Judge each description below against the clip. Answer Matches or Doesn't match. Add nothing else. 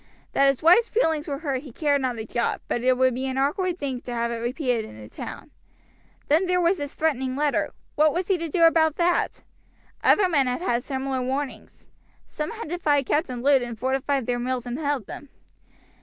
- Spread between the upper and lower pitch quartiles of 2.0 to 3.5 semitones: Doesn't match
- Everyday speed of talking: Doesn't match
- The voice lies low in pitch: Doesn't match